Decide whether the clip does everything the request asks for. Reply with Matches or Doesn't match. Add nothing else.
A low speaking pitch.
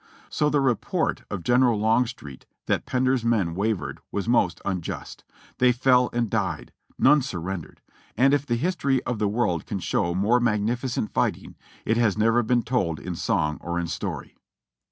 Matches